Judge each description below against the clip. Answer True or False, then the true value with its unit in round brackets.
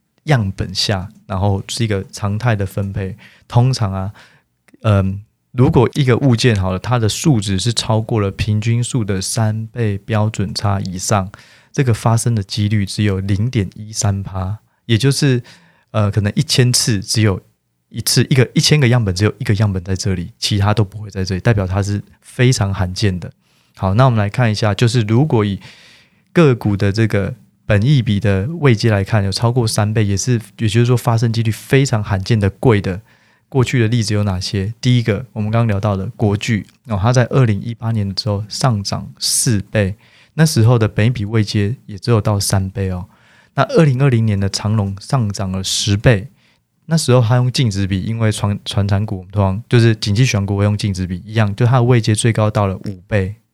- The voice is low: True (110 Hz)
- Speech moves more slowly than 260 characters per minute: False (290 characters per minute)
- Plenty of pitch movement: False (3.1 semitones)